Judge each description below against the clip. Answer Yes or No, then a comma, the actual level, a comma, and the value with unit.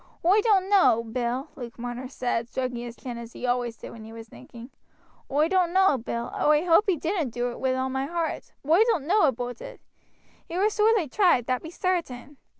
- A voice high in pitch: Yes, very high, 265 Hz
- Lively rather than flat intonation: Yes, wide, 6.6 semitones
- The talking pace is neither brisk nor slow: No, fast, 215 wpm